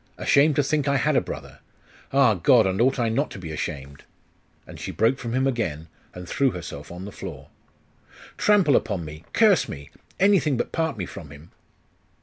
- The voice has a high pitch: No, low, 115 Hz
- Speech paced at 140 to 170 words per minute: No, average, 195 wpm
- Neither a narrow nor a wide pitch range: No, wide, 8.5 semitones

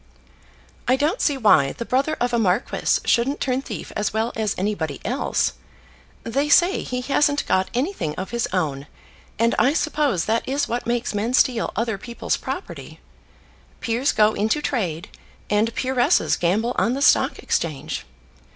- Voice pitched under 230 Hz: No, high, 235 Hz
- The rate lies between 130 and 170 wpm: Yes, average, 160 wpm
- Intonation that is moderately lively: Yes, average, 4.4 semitones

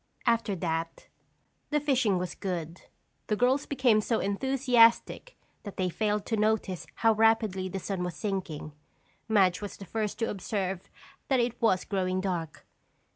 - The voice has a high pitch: Yes, high, 205 Hz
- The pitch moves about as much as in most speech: Yes, average, 3.6 semitones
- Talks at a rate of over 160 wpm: No, average, 150 wpm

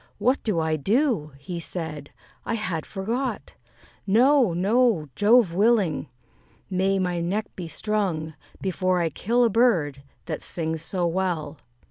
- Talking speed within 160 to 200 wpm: No, slow, 135 wpm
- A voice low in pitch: No, medium, 185 Hz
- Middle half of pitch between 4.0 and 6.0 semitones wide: Yes, average, 5.2 semitones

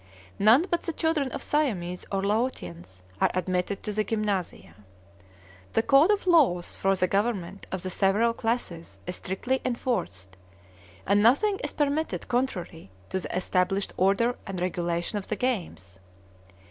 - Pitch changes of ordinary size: No, wide, 5.7 semitones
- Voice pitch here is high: Yes, high, 200 Hz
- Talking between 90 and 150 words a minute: Yes, average, 145 wpm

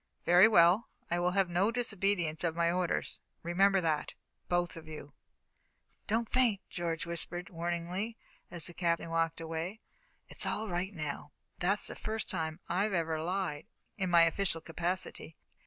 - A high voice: No, medium, 175 Hz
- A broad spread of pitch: No, average, 2.9 semitones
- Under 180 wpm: Yes, average, 155 wpm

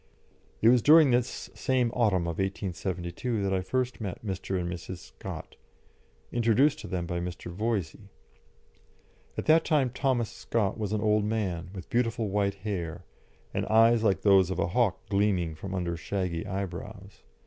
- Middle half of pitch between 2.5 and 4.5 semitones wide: Yes, average, 4.1 semitones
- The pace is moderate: Yes, average, 160 wpm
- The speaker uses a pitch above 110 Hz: No, low, 100 Hz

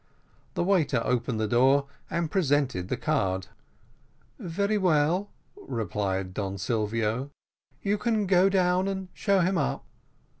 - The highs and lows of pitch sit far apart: Yes, wide, 8.9 semitones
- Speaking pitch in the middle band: Yes, medium, 145 Hz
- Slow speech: Yes, slow, 125 wpm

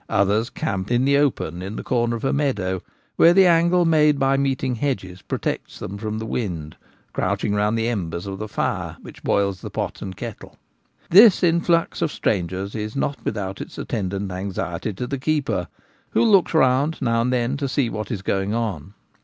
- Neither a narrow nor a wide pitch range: No, wide, 6.2 semitones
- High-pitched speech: No, low, 115 Hz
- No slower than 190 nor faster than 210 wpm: Yes, average, 195 wpm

